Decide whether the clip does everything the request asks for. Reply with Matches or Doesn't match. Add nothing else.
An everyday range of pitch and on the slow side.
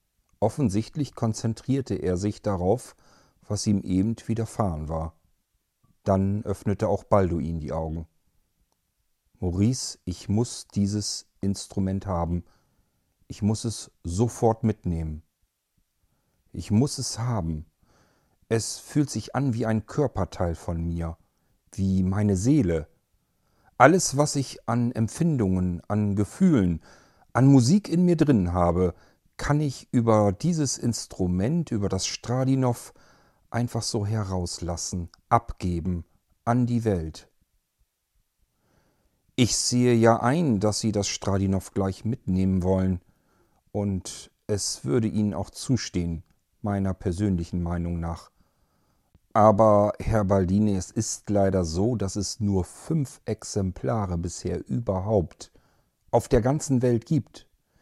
Matches